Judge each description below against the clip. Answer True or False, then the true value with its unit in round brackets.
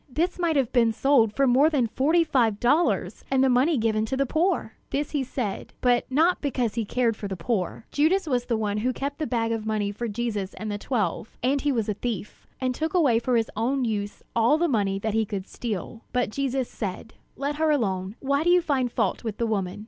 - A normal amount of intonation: True (4.3 semitones)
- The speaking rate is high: True (230 wpm)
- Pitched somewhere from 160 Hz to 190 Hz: False (245 Hz)